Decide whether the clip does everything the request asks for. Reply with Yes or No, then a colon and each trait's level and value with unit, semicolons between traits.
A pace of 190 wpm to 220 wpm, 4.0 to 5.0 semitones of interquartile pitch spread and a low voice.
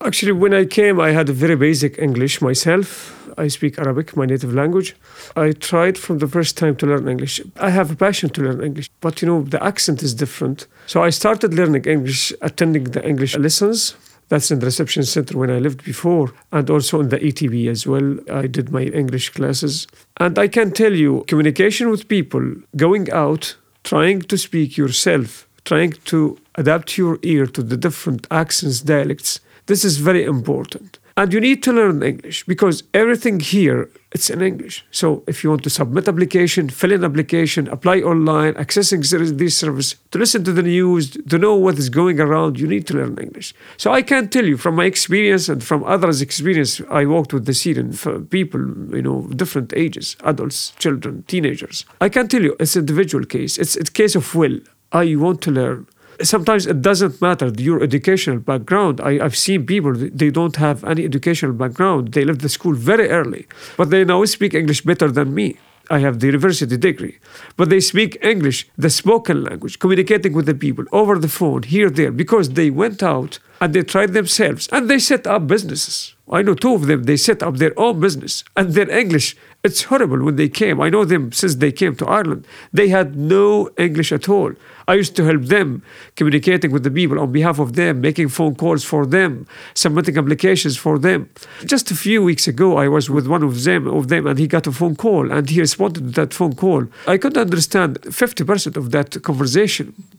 No: average, 200 wpm; average, 4.5 semitones; medium, 165 Hz